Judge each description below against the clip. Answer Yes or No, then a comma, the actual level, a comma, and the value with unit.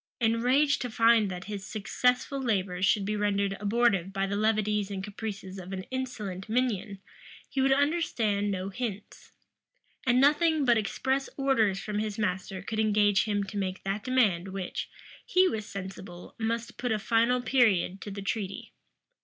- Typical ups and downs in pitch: Yes, average, 3.7 semitones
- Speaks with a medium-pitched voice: No, high, 210 Hz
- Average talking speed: Yes, average, 160 wpm